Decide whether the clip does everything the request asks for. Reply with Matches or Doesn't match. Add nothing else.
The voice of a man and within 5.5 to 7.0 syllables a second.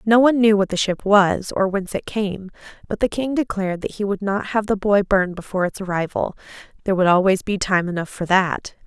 Doesn't match